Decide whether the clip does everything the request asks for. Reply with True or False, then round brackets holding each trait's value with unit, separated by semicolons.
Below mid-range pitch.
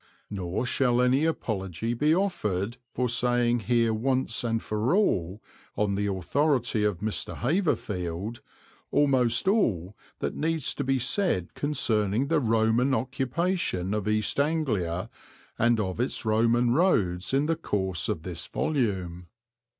True (115 Hz)